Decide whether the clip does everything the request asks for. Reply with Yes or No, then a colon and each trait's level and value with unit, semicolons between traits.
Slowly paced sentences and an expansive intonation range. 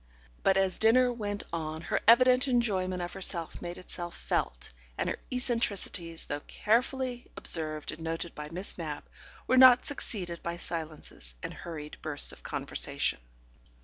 No: average, 145 wpm; wide, 6.3 semitones